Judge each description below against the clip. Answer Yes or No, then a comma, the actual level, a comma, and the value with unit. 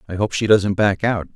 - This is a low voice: Yes, low, 100 Hz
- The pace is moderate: No, fast, 265 wpm